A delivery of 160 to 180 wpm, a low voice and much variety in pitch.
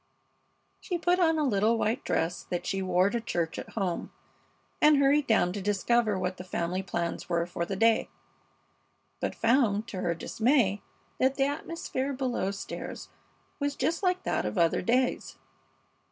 No: average, 165 wpm; high, 220 Hz; wide, 6.9 semitones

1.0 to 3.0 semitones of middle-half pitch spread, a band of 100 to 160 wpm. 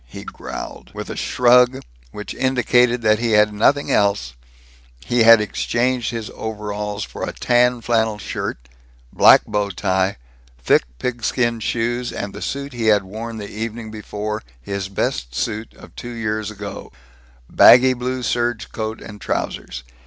Yes: narrow, 2.6 semitones; average, 150 wpm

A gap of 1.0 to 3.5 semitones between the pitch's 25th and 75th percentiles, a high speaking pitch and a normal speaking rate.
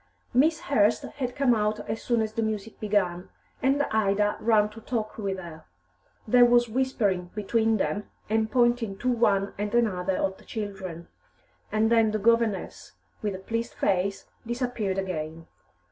Yes: average, 3.1 semitones; high, 215 Hz; average, 160 wpm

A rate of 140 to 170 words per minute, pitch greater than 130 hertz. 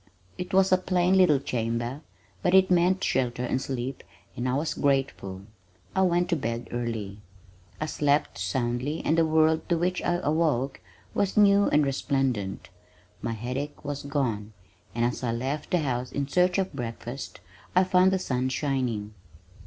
Yes: average, 165 wpm; medium, 140 Hz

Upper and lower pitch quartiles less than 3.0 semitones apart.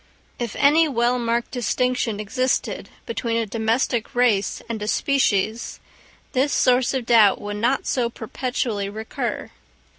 Yes: narrow, 2.5 semitones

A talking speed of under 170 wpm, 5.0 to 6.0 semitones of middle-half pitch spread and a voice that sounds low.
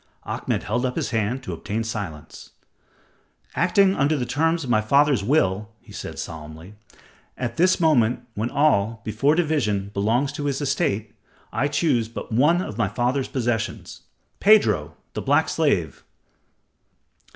Yes: average, 145 wpm; average, 5.3 semitones; low, 125 Hz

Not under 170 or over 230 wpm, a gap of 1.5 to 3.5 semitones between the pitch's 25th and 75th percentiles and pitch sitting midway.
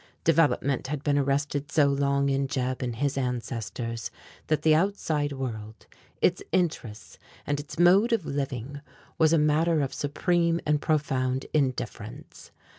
No: average, 140 wpm; average, 3.1 semitones; medium, 145 Hz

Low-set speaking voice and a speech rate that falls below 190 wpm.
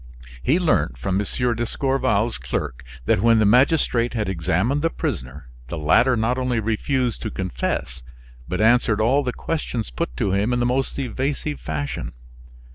Yes: low, 115 Hz; average, 160 wpm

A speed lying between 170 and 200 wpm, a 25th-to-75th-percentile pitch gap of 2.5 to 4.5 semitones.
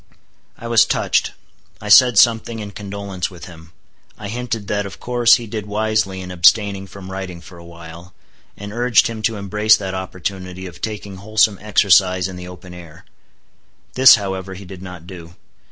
Yes: average, 175 wpm; average, 2.8 semitones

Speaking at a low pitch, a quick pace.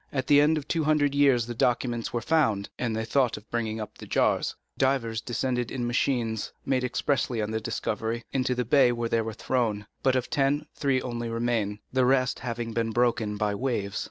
Yes: low, 120 Hz; fast, 210 wpm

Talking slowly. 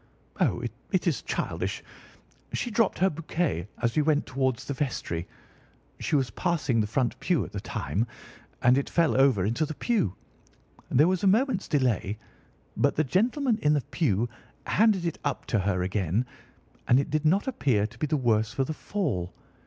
No: average, 180 wpm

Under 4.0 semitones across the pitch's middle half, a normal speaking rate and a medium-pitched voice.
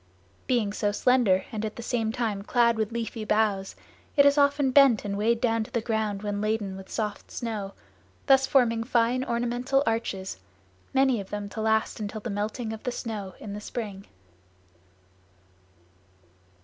No: average, 2.7 semitones; average, 165 wpm; high, 220 Hz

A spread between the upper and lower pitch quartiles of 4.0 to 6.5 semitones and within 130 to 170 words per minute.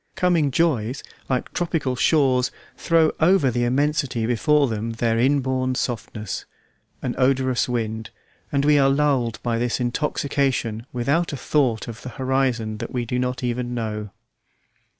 No: average, 3.2 semitones; average, 145 wpm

